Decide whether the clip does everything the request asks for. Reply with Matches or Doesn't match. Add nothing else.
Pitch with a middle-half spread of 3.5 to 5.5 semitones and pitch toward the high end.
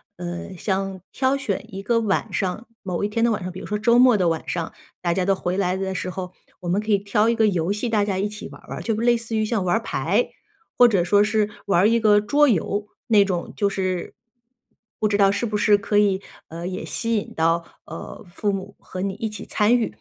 Doesn't match